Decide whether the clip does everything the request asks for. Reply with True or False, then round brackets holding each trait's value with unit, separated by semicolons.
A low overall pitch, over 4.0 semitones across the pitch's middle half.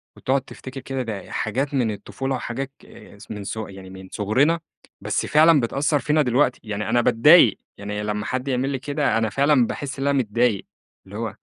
True (125 Hz; 4.6 semitones)